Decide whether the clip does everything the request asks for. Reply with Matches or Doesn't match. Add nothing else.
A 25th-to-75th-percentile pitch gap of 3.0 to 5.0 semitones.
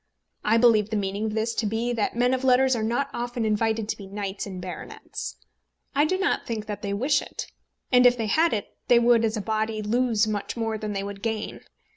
Doesn't match